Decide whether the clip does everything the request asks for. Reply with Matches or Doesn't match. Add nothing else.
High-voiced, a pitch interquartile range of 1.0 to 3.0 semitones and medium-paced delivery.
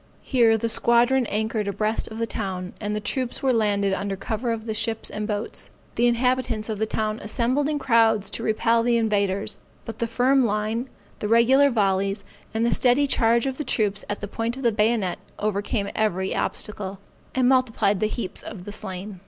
Matches